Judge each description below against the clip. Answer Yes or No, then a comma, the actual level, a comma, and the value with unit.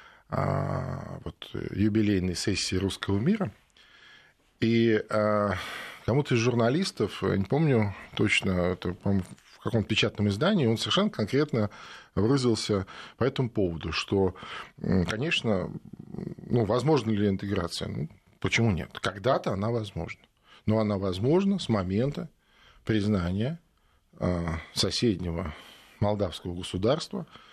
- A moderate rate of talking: No, slow, 105 wpm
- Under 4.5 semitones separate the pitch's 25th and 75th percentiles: Yes, average, 3.3 semitones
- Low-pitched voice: Yes, low, 105 Hz